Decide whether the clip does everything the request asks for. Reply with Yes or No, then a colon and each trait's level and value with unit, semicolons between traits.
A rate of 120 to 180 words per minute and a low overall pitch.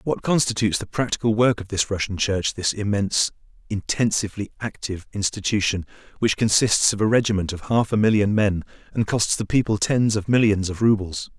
Yes: average, 175 wpm; low, 105 Hz